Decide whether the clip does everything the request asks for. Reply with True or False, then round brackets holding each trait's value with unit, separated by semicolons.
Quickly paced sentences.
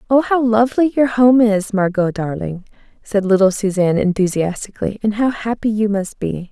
False (165 wpm)